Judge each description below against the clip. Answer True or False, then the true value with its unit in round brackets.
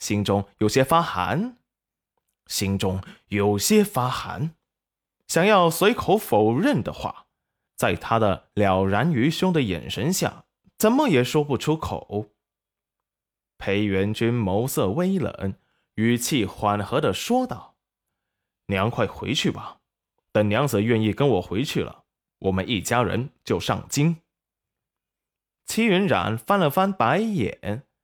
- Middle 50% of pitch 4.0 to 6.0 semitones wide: False (7.7 semitones)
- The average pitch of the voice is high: False (120 Hz)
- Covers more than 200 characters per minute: False (180 characters per minute)